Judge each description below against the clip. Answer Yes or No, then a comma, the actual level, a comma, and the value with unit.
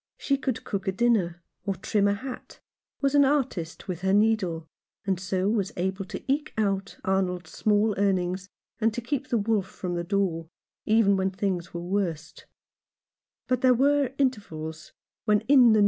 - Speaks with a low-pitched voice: No, high, 200 Hz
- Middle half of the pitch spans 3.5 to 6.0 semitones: Yes, average, 4.1 semitones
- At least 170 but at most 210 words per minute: Yes, average, 180 wpm